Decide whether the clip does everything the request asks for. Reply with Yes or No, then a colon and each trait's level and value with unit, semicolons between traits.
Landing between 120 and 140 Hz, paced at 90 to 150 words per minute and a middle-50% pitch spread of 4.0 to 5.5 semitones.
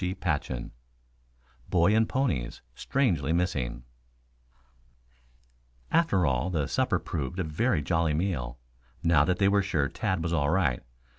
No: very low, 85 Hz; slow, 135 wpm; average, 4.9 semitones